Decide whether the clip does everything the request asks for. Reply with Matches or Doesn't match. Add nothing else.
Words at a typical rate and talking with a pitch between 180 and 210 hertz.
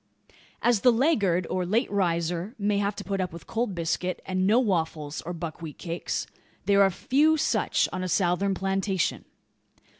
Matches